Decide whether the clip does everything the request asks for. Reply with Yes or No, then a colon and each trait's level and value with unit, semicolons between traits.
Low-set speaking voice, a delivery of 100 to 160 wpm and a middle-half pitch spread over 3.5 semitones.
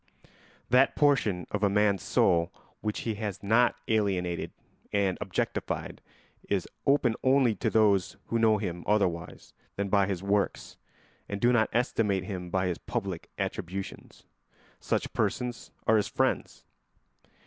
No: low, 100 Hz; slow, 135 wpm; average, 3.0 semitones